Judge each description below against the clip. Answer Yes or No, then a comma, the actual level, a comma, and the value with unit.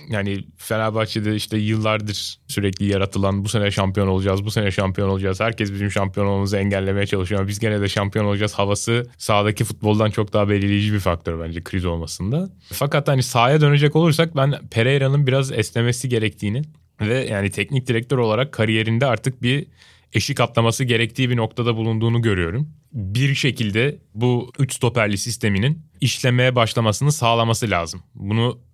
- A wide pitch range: No, average, 3.7 semitones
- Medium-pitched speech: No, low, 110 Hz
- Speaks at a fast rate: Yes, fast, 150 wpm